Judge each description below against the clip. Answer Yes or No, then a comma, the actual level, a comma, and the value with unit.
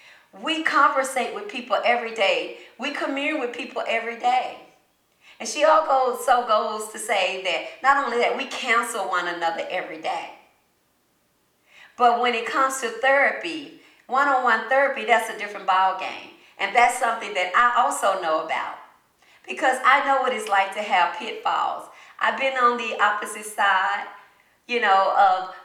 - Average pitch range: Yes, average, 5.0 semitones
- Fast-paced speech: No, average, 160 wpm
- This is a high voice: Yes, high, 240 Hz